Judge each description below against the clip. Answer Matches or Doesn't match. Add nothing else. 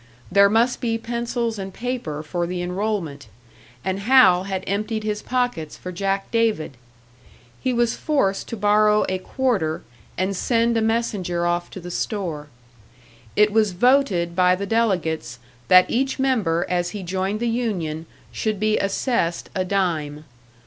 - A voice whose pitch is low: Doesn't match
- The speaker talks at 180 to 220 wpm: Doesn't match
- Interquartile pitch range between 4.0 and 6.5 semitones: Matches